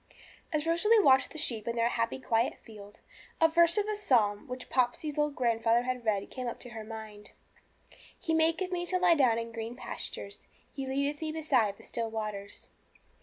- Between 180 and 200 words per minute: Yes, average, 185 wpm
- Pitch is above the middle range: Yes, very high, 250 Hz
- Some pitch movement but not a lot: No, wide, 5.8 semitones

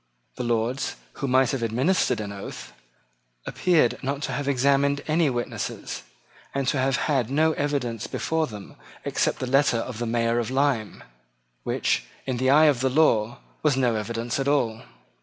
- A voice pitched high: No, low, 130 Hz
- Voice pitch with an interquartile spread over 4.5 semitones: No, average, 3.3 semitones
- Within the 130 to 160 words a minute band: No, average, 170 wpm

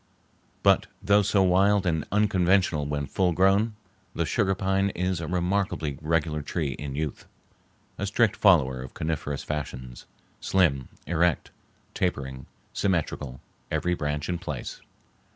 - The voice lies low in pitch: Yes, very low, 85 Hz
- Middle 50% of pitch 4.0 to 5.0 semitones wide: Yes, average, 4.6 semitones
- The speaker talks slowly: Yes, slow, 130 wpm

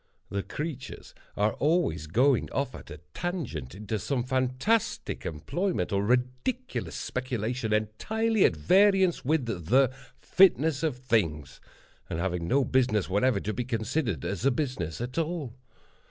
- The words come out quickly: No, average, 140 wpm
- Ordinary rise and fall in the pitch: No, wide, 6.8 semitones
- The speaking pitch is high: No, low, 125 Hz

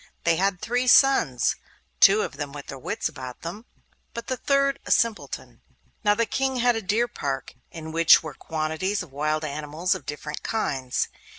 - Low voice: No, medium, 170 Hz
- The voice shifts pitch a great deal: Yes, wide, 7.4 semitones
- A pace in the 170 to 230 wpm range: Yes, average, 180 wpm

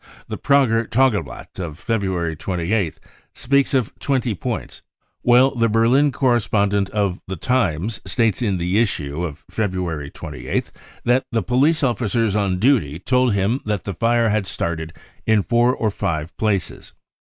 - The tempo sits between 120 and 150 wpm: Yes, average, 145 wpm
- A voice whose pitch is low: Yes, low, 110 Hz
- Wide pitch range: No, average, 4.8 semitones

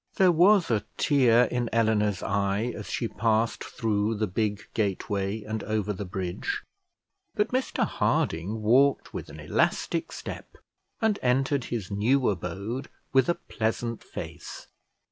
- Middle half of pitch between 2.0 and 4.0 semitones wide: Yes, average, 3.5 semitones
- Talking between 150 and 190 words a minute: No, average, 140 wpm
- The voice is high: No, low, 110 Hz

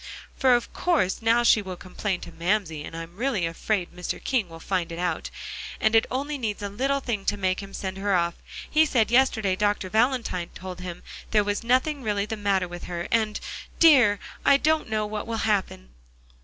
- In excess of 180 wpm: Yes, average, 200 wpm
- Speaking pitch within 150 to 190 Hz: No, high, 205 Hz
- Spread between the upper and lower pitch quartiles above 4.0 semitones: Yes, average, 4.5 semitones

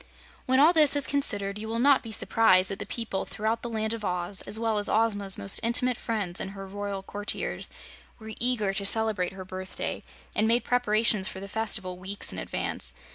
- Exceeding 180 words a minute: Yes, average, 200 wpm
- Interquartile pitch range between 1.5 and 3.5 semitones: Yes, average, 2.8 semitones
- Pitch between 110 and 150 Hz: No, high, 215 Hz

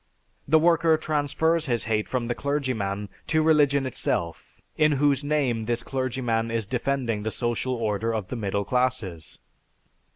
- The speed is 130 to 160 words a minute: Yes, average, 150 wpm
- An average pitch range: Yes, average, 4.5 semitones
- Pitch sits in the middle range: No, low, 125 Hz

